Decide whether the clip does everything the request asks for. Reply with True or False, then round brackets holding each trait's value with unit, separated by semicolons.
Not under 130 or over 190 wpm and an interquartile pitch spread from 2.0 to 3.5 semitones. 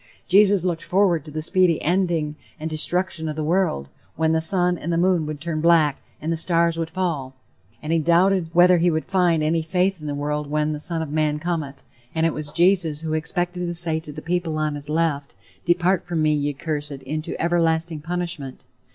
False (205 wpm; 2.4 semitones)